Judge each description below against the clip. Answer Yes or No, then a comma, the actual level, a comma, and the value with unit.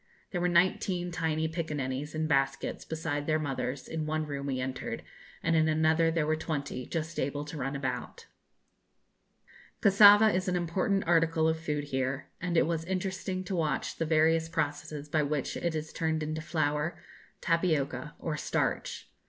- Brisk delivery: No, average, 165 wpm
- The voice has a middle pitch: Yes, medium, 160 Hz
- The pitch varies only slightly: Yes, narrow, 2.3 semitones